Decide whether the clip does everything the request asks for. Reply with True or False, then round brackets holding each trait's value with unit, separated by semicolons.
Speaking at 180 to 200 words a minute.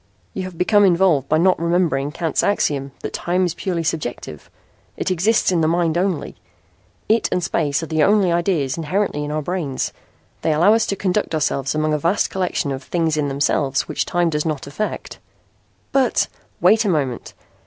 True (185 wpm)